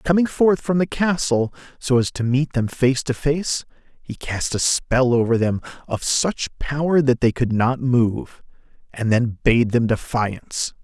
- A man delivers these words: Yes, male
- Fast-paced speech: No, average, 175 wpm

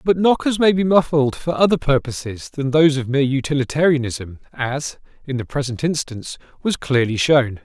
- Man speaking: Yes, male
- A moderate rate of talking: Yes, average, 165 wpm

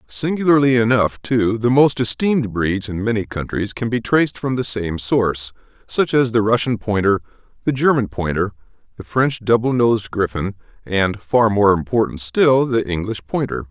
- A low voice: Yes, low, 115 Hz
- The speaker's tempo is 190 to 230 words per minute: No, average, 165 wpm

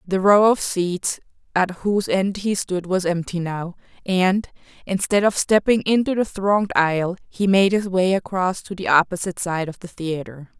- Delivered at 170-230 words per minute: Yes, average, 180 wpm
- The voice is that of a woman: Yes, female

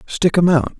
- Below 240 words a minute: Yes, fast, 225 wpm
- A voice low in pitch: No, medium, 165 Hz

